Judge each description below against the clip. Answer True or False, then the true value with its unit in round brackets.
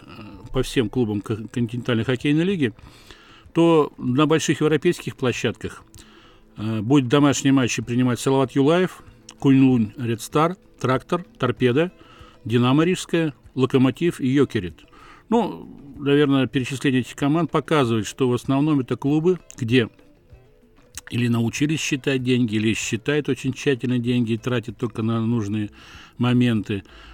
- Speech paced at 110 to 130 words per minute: True (120 wpm)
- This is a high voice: False (130 Hz)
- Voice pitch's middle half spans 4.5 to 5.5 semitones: False (3.9 semitones)